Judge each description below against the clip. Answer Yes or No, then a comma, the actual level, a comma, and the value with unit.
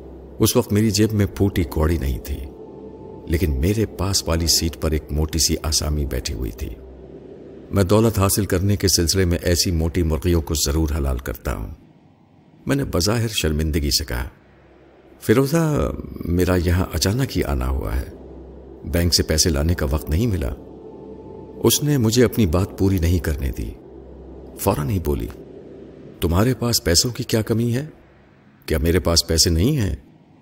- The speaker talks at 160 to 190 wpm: Yes, average, 165 wpm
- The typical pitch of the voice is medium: No, very low, 85 Hz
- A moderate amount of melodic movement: Yes, average, 5.0 semitones